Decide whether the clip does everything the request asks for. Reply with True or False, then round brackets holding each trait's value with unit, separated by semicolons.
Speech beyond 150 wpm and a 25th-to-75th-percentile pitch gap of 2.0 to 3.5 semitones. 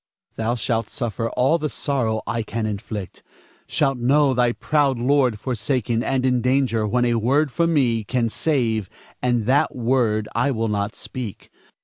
True (160 wpm; 3.1 semitones)